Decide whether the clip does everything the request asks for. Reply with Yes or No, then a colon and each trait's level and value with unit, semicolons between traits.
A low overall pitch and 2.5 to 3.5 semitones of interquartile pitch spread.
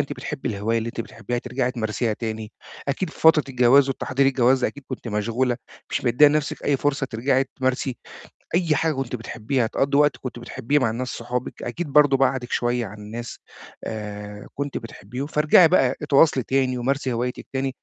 Yes: low, 130 Hz; average, 2.9 semitones